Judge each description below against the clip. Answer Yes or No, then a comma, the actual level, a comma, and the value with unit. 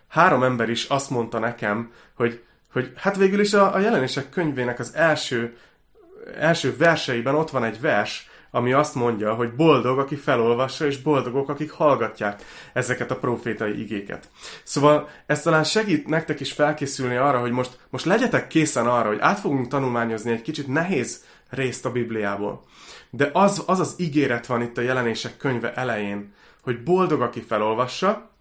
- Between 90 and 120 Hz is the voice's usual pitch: No, low, 130 Hz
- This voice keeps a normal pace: No, fast, 165 wpm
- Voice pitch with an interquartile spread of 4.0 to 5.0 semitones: Yes, average, 4.6 semitones